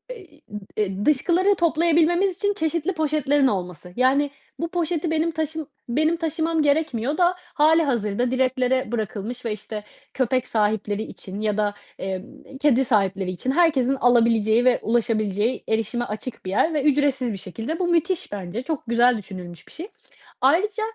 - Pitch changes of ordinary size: No, wide, 6.7 semitones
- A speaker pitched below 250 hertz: No, very high, 260 Hz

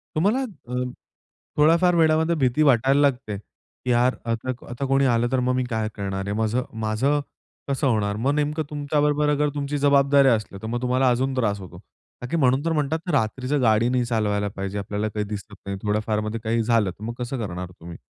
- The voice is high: No, low, 125 Hz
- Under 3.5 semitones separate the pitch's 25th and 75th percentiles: No, average, 4.9 semitones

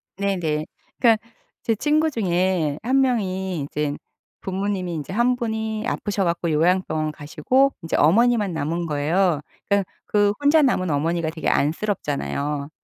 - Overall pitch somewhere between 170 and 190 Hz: Yes, medium, 185 Hz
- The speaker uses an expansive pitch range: Yes, wide, 6.0 semitones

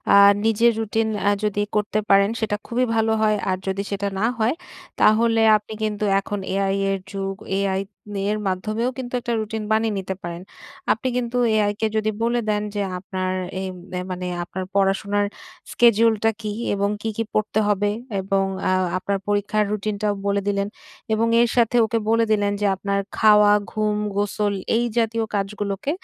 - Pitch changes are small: Yes, narrow, 1.9 semitones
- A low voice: No, high, 210 Hz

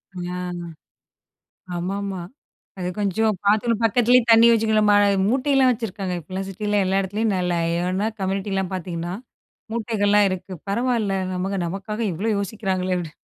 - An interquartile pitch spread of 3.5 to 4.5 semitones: No, average, 2.9 semitones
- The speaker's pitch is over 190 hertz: Yes, high, 200 Hz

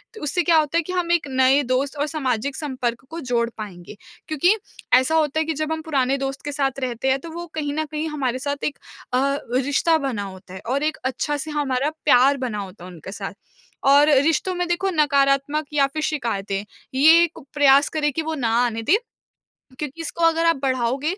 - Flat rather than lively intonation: No, average, 3.4 semitones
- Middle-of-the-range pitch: No, very high, 280 Hz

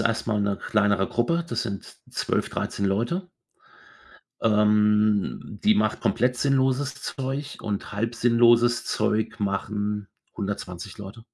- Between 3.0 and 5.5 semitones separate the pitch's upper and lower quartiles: No, narrow, 2.6 semitones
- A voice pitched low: Yes, low, 110 Hz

